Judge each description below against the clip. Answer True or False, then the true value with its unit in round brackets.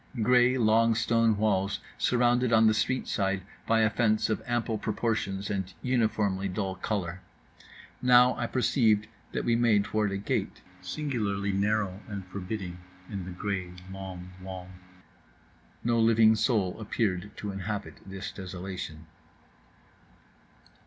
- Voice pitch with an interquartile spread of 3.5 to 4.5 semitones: False (3.0 semitones)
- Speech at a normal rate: False (130 wpm)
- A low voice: True (105 Hz)